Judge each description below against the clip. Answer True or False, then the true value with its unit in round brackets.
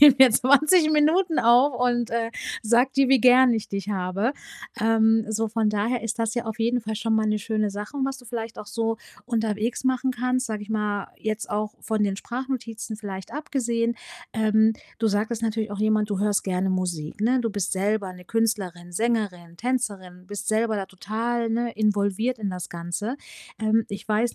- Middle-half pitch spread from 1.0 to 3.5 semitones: True (2.6 semitones)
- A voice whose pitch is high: True (220 Hz)